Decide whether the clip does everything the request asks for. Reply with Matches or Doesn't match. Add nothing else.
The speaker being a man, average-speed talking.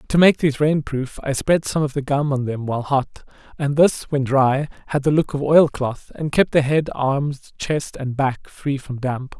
Doesn't match